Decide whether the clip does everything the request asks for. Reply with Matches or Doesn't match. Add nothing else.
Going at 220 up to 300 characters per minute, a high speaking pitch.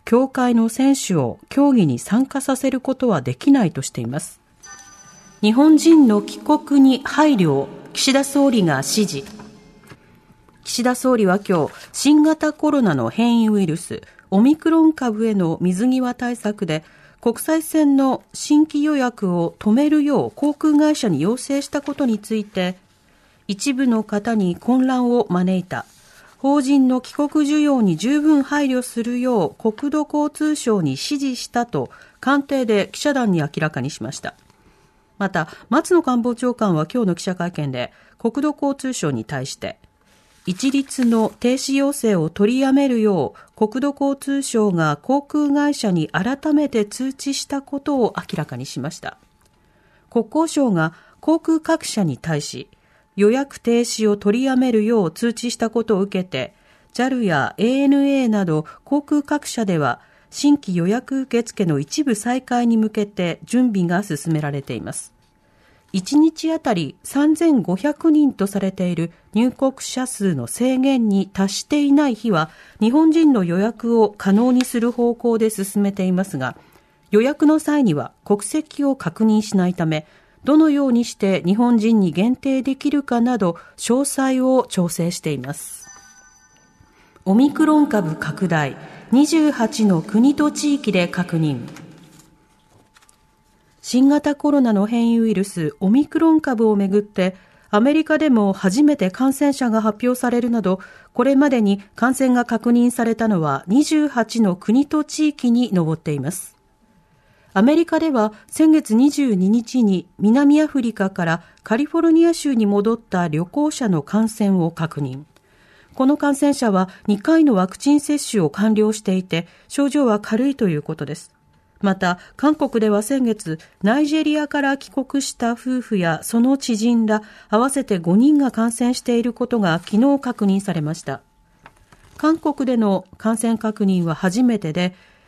Matches